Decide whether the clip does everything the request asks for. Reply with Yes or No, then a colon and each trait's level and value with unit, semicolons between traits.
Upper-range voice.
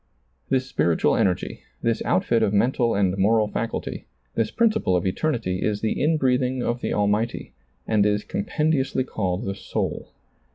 No: low, 110 Hz